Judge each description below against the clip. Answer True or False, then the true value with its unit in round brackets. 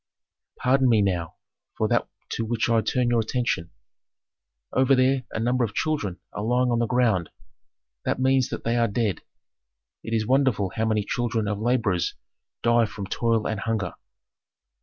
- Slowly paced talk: False (165 wpm)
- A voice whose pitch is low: True (115 Hz)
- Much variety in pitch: False (3.0 semitones)